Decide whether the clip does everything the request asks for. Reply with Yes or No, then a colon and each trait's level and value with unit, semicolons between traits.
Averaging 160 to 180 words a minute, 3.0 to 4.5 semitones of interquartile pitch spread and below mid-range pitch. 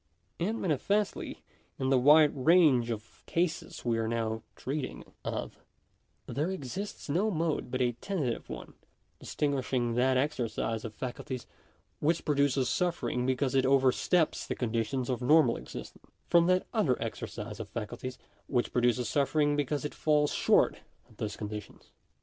No: average, 150 wpm; average, 4.1 semitones; low, 130 Hz